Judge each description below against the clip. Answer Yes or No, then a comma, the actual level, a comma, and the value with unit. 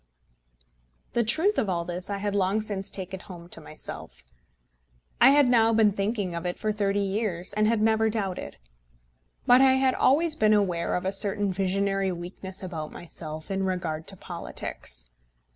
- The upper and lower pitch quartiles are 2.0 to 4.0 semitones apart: Yes, average, 3.3 semitones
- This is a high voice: Yes, high, 195 Hz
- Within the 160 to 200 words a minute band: Yes, average, 170 wpm